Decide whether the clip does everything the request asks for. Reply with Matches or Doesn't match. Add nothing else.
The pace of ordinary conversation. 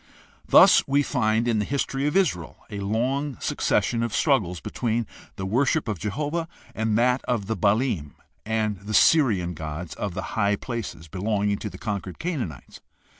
Matches